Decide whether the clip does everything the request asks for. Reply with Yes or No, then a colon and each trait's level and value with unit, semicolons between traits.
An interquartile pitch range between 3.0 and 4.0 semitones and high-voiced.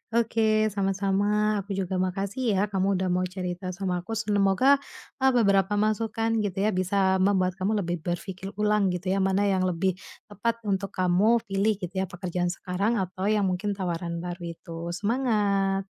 No: narrow, 2.4 semitones; high, 195 Hz